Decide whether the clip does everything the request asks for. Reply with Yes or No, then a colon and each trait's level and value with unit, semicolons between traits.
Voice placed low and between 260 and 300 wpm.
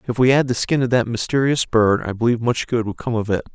Yes: low, 120 Hz; fast, 285 wpm